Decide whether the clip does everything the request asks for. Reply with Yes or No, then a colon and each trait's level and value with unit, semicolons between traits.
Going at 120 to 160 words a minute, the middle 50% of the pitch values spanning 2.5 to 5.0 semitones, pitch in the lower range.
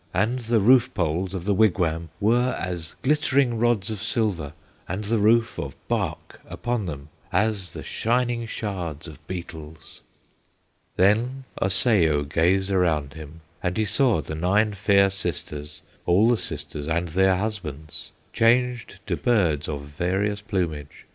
No: average, 140 wpm; wide, 5.4 semitones; very low, 95 Hz